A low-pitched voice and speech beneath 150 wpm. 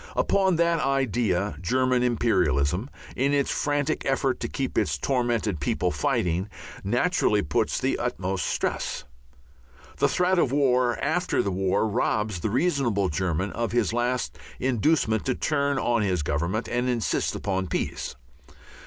Yes: low, 120 Hz; average, 140 wpm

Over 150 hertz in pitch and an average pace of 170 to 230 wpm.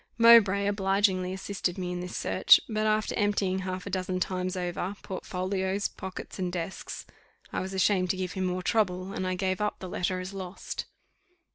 Yes: medium, 185 Hz; average, 180 wpm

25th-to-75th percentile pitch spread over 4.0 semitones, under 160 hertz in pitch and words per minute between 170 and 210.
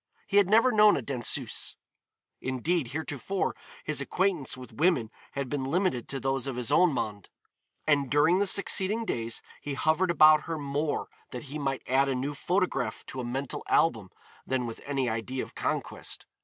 Yes: average, 5.1 semitones; medium, 140 Hz; average, 175 wpm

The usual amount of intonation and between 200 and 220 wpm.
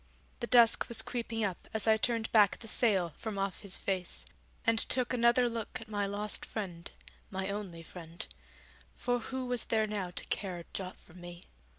No: average, 3.7 semitones; average, 190 wpm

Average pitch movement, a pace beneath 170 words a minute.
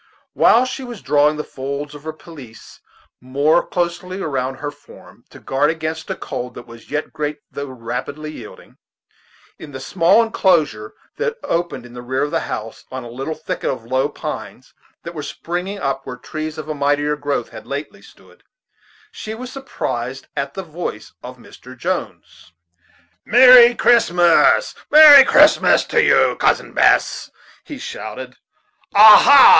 No: wide, 5.7 semitones; average, 160 wpm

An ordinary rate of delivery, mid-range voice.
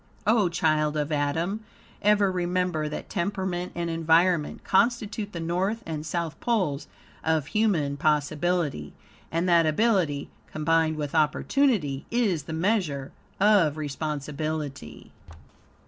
No: slow, 115 wpm; medium, 165 Hz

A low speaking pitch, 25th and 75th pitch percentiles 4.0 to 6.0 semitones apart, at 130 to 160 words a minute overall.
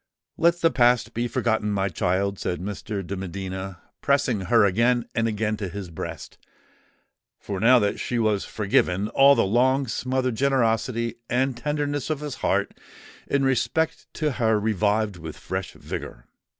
Yes: low, 110 Hz; average, 4.5 semitones; average, 155 wpm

